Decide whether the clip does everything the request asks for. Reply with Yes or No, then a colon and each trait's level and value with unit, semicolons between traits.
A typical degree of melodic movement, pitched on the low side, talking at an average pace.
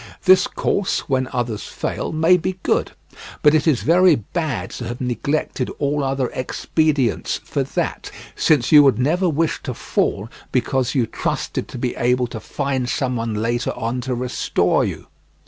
Yes: average, 4.2 semitones; low, 130 Hz; average, 165 wpm